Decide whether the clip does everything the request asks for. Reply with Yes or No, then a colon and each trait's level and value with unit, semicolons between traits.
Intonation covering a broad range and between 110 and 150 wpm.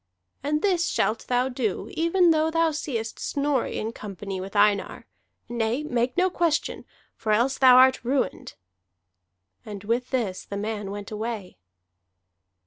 Yes: wide, 5.7 semitones; average, 140 wpm